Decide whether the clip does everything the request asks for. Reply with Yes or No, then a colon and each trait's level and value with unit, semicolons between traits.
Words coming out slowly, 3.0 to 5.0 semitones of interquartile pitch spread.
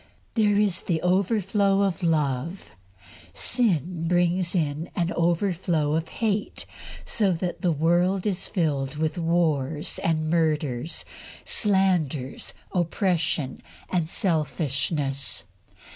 Yes: slow, 100 wpm; average, 3.4 semitones